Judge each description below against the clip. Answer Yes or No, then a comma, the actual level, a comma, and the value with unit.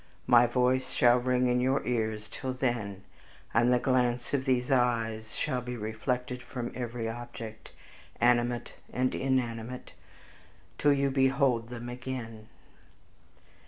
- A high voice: No, low, 125 Hz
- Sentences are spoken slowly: Yes, slow, 125 wpm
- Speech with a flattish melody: Yes, narrow, 1.6 semitones